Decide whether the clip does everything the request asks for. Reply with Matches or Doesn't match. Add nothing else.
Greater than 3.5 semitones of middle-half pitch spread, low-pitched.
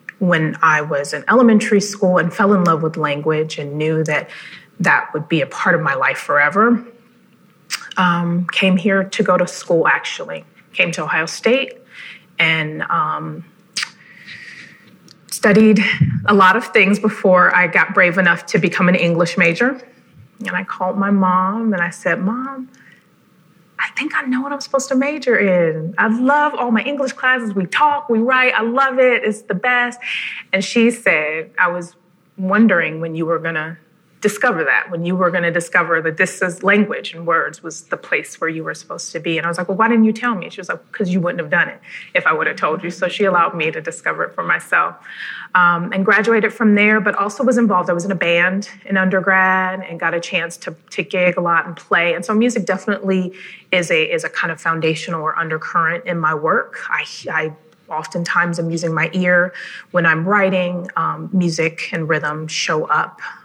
Doesn't match